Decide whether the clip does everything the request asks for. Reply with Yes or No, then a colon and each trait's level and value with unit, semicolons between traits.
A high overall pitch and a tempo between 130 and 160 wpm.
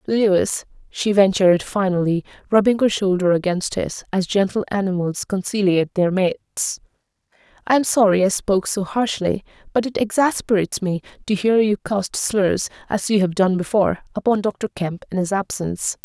Yes: high, 195 Hz; average, 155 wpm